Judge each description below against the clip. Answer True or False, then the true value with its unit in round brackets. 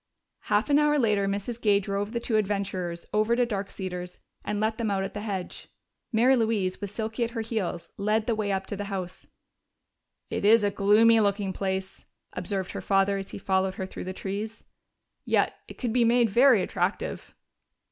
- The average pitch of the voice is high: True (205 Hz)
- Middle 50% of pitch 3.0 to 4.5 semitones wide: False (2.6 semitones)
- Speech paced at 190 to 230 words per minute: True (195 wpm)